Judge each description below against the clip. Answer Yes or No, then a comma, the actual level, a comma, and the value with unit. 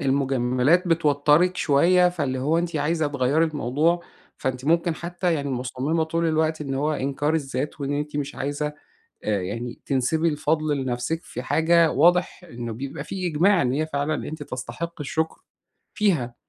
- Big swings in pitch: No, average, 3.6 semitones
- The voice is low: No, medium, 150 Hz